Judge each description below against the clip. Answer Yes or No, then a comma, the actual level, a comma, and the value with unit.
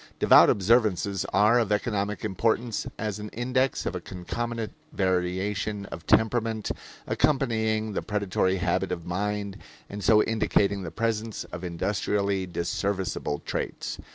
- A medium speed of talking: No, slow, 125 wpm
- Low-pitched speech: Yes, low, 105 Hz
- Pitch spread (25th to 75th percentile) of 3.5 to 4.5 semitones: No, average, 2.7 semitones